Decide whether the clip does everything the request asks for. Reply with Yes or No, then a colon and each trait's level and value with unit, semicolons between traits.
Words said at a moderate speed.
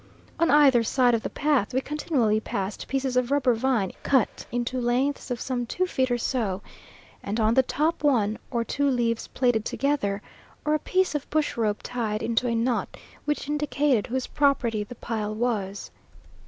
Yes: average, 180 wpm